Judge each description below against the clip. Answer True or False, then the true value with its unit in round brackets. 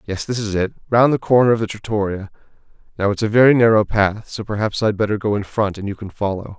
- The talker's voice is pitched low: True (105 Hz)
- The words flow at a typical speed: False (265 wpm)